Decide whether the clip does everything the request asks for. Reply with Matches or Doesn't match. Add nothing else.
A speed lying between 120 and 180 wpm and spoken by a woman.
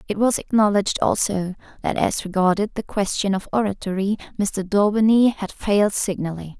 Matches